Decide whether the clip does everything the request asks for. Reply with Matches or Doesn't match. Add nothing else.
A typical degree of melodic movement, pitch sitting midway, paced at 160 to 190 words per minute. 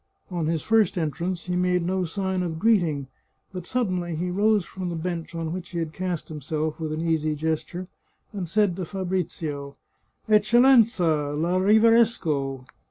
Matches